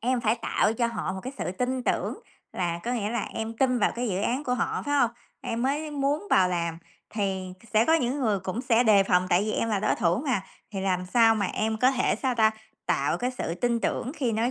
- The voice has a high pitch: Yes, high, 225 Hz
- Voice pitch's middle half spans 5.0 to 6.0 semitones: No, average, 4.3 semitones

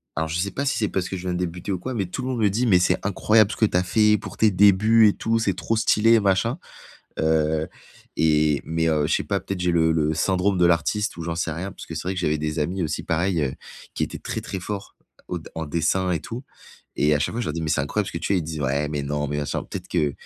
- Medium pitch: No, very low, 90 Hz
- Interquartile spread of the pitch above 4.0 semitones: Yes, average, 4.4 semitones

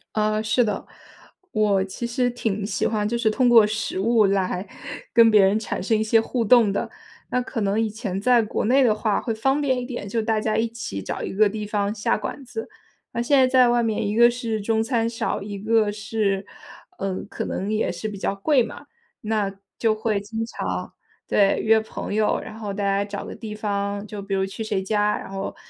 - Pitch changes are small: Yes, narrow, 2.3 semitones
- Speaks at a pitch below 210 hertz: No, high, 215 Hz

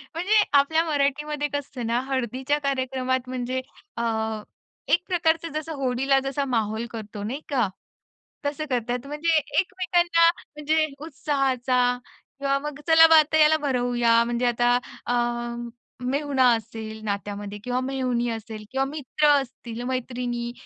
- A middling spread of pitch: Yes, average, 3.7 semitones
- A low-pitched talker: No, very high, 260 Hz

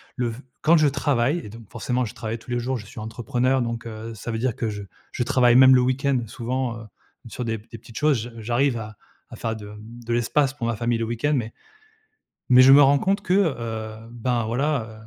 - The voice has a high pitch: No, low, 120 Hz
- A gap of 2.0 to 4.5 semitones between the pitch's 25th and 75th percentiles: Yes, average, 2.7 semitones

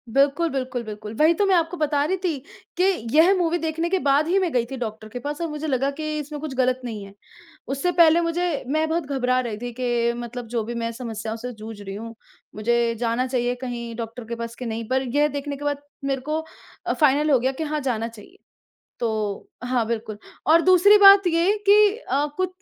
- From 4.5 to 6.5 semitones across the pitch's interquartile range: Yes, average, 5.3 semitones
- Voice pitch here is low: No, very high, 270 Hz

